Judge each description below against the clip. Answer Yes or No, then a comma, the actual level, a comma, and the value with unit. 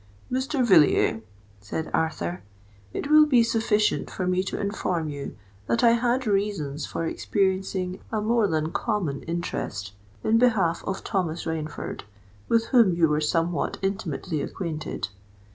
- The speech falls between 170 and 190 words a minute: No, average, 140 wpm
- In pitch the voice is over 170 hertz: Yes, medium, 185 Hz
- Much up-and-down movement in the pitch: Yes, wide, 5.8 semitones